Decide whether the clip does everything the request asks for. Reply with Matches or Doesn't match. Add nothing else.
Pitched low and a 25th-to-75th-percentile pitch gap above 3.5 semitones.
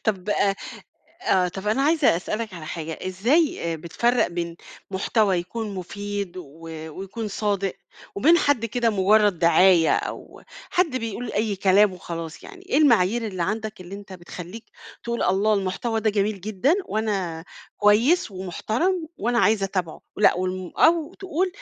Doesn't match